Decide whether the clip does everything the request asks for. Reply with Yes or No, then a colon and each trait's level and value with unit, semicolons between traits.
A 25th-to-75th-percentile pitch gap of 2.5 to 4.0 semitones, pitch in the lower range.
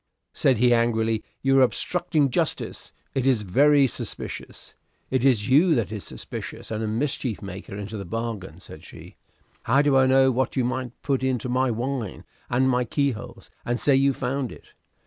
Yes: average, 3.1 semitones; low, 125 Hz